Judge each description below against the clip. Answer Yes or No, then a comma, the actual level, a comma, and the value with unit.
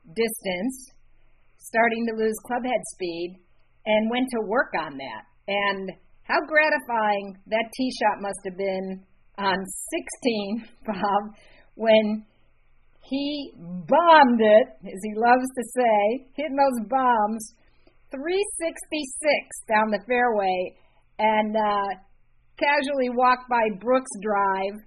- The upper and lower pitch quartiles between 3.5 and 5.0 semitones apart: Yes, average, 4.3 semitones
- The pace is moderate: No, slow, 115 wpm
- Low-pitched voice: No, high, 225 Hz